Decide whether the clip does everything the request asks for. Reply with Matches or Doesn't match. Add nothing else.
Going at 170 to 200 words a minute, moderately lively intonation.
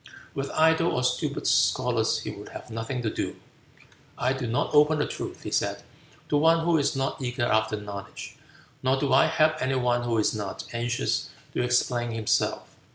Matches